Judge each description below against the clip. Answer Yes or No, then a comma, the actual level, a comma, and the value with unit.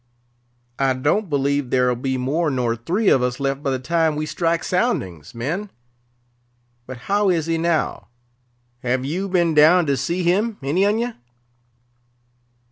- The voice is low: No, medium, 150 Hz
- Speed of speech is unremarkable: Yes, average, 155 wpm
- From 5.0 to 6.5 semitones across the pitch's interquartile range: Yes, wide, 5.4 semitones